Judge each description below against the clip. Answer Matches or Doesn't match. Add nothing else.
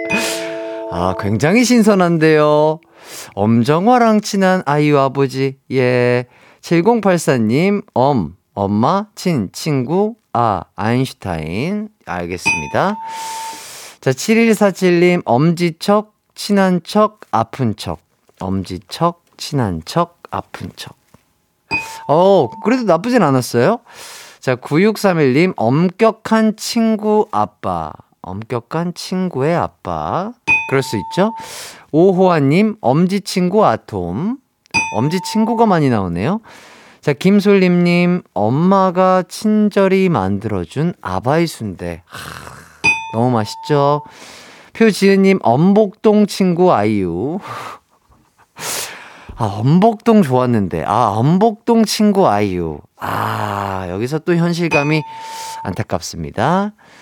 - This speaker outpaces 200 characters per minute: Doesn't match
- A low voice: Doesn't match